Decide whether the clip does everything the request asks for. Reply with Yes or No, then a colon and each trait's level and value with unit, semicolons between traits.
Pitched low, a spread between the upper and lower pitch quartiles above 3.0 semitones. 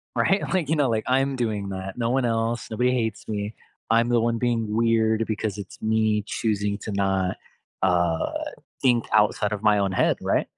No: low, 110 Hz; narrow, 2.5 semitones